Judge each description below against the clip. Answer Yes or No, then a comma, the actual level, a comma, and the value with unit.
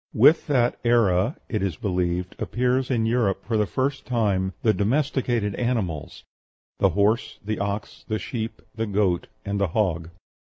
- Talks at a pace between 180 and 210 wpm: No, average, 155 wpm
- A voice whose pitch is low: Yes, low, 110 Hz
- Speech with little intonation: No, average, 3.8 semitones